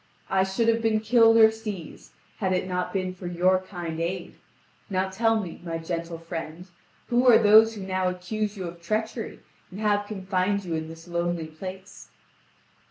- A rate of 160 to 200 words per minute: Yes, average, 175 wpm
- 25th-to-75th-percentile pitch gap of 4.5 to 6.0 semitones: No, average, 3.6 semitones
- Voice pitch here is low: No, high, 190 Hz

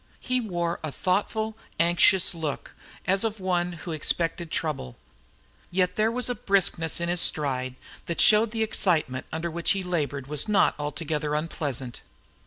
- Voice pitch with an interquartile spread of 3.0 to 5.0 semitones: Yes, average, 4.5 semitones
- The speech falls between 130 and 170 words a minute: Yes, average, 155 wpm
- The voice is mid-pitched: Yes, medium, 170 Hz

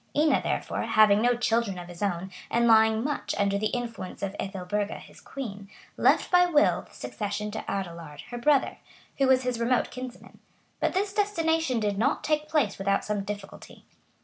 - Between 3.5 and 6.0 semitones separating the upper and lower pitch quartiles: Yes, average, 5.0 semitones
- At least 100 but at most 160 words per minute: No, average, 175 wpm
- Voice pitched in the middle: No, high, 220 Hz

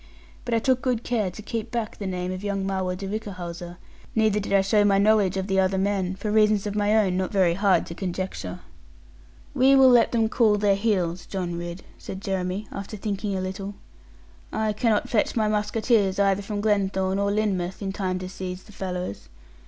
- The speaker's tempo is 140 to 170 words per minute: No, average, 200 wpm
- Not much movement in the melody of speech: Yes, narrow, 2.2 semitones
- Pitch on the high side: Yes, high, 200 Hz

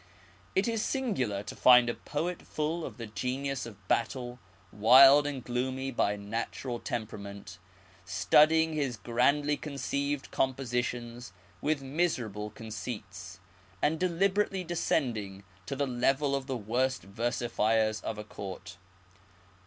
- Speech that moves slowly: Yes, slow, 125 wpm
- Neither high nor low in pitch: No, low, 125 Hz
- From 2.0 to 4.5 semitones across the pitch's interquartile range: No, average, 4.9 semitones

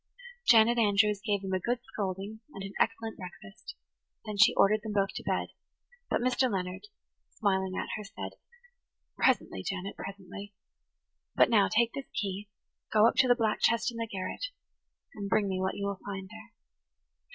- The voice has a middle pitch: No, high, 205 Hz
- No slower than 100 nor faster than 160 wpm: No, average, 175 wpm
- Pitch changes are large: No, narrow, 2.6 semitones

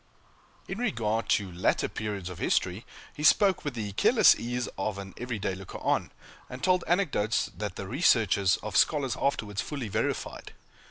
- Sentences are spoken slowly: No, average, 165 wpm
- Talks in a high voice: No, low, 110 Hz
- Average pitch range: No, wide, 6.3 semitones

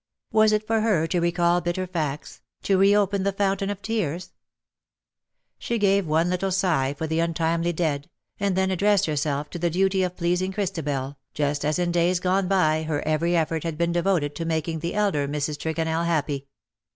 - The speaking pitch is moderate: Yes, medium, 170 Hz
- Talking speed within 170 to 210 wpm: Yes, average, 190 wpm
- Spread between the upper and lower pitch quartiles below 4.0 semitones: Yes, average, 3.5 semitones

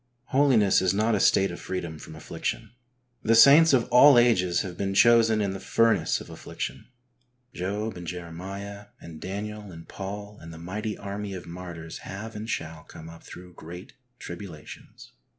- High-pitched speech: No, very low, 95 Hz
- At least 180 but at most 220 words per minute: No, average, 170 wpm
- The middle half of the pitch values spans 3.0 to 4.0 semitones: Yes, average, 3.6 semitones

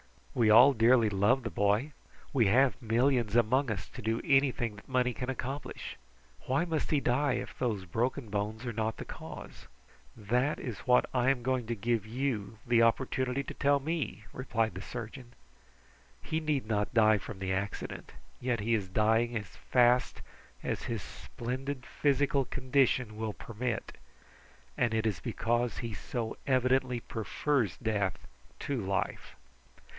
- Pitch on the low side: Yes, low, 120 Hz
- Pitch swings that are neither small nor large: Yes, average, 3.2 semitones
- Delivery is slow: No, average, 155 wpm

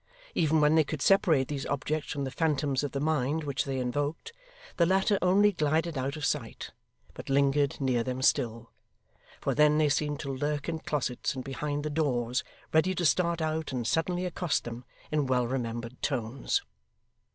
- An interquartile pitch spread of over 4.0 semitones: No, average, 3.2 semitones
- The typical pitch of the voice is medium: Yes, medium, 145 Hz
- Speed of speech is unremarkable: Yes, average, 180 wpm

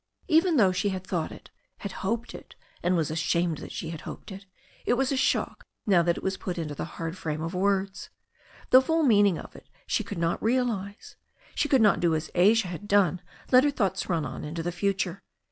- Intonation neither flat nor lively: Yes, average, 4.5 semitones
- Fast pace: Yes, fast, 220 wpm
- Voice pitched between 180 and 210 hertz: Yes, high, 190 Hz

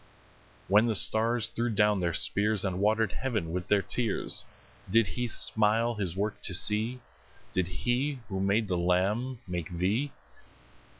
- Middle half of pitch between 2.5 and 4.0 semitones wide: Yes, average, 3.6 semitones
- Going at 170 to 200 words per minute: No, average, 155 wpm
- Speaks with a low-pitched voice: Yes, low, 105 Hz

